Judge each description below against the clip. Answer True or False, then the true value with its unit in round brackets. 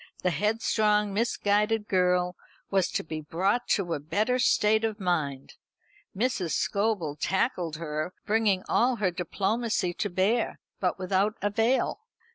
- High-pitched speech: True (195 Hz)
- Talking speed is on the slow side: True (130 wpm)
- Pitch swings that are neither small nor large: True (3.5 semitones)